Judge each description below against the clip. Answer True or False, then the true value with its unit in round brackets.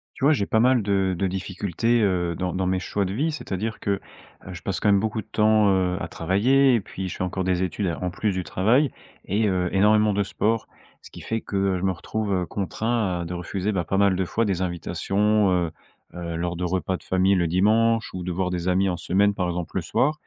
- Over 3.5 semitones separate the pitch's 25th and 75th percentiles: False (2.9 semitones)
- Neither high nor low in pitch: False (95 Hz)